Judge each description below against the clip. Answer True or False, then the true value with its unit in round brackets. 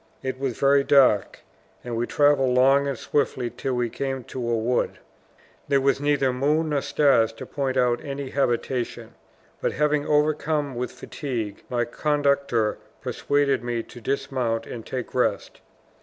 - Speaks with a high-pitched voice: False (135 Hz)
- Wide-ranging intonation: False (2.7 semitones)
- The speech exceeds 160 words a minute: False (155 wpm)